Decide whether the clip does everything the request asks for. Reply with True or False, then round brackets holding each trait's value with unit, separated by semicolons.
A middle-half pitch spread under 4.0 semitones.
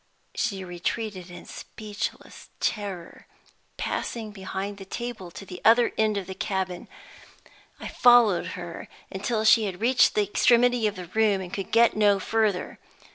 True (2.9 semitones)